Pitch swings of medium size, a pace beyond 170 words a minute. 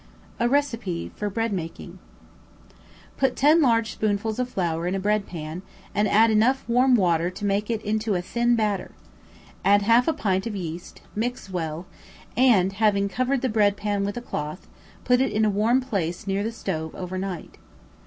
Yes: average, 3.9 semitones; average, 180 wpm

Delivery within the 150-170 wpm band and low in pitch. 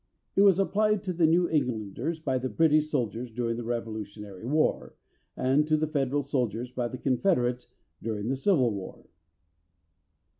Yes: average, 155 wpm; low, 130 Hz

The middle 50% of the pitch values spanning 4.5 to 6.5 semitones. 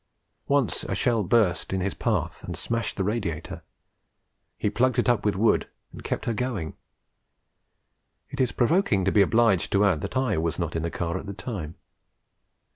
Yes: average, 4.8 semitones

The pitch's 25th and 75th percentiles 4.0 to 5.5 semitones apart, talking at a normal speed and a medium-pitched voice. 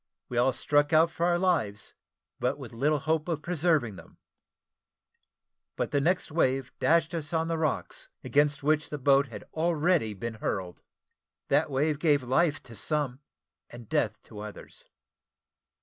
Yes: average, 4.4 semitones; average, 155 wpm; medium, 145 Hz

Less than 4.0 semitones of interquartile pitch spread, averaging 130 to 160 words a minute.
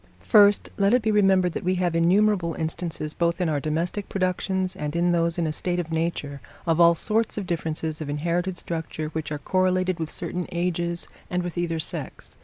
No: narrow, 2.4 semitones; average, 200 wpm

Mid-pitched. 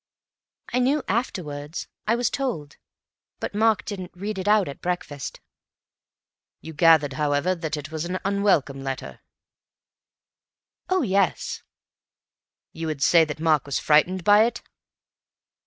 Yes: medium, 175 Hz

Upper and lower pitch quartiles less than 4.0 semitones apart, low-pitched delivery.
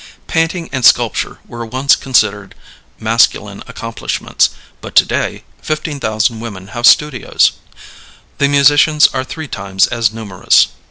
No: average, 4.8 semitones; low, 120 Hz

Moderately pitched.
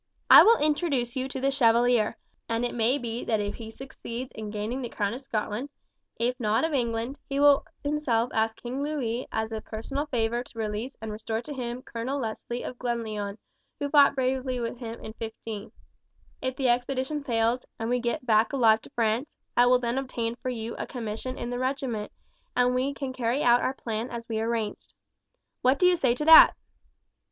No: high, 240 Hz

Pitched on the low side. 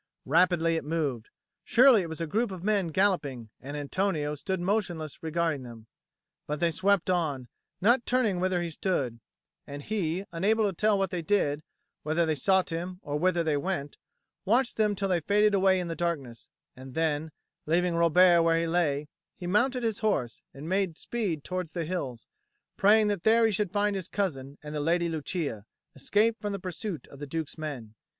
No: medium, 170 Hz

